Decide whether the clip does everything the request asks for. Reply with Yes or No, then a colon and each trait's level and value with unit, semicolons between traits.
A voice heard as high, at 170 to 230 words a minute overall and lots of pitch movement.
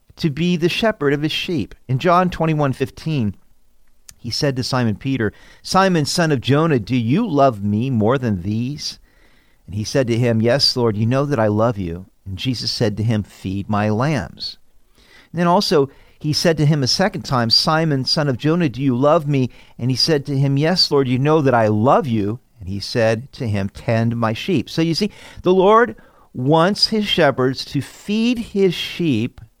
No: low, 135 Hz; average, 200 wpm; wide, 5.8 semitones